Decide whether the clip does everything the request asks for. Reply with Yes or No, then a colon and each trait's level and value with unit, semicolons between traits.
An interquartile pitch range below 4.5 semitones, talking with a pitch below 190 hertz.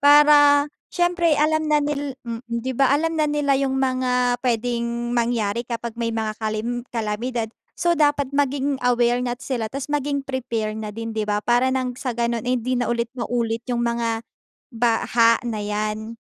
No: average, 3.3 semitones; high, 245 Hz